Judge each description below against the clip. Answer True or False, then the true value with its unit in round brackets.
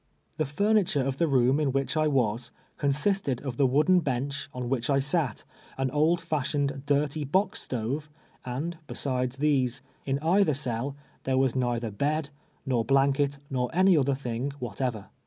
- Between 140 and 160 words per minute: True (155 wpm)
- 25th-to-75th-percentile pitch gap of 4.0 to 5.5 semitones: False (3.0 semitones)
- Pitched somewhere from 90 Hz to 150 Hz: True (140 Hz)